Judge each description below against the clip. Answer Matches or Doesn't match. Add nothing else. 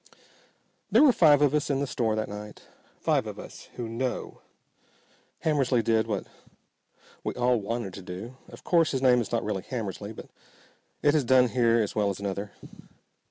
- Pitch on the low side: Matches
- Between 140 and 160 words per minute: Doesn't match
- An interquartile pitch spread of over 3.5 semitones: Matches